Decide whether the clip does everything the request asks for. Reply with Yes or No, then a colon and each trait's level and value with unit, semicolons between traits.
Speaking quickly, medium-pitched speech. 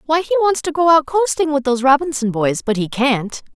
No: fast, 235 wpm; very high, 275 Hz